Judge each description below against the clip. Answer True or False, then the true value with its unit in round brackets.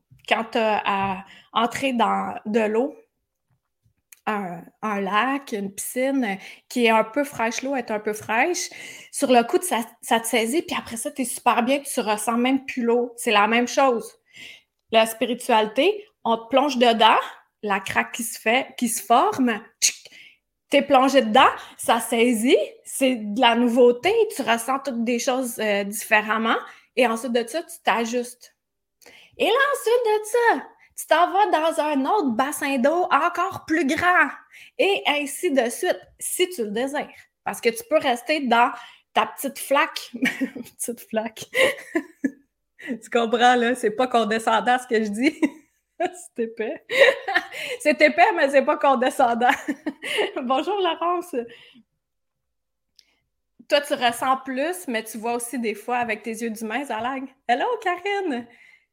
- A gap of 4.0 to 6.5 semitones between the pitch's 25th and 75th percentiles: True (4.7 semitones)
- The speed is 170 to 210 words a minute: False (160 wpm)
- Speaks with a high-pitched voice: True (255 Hz)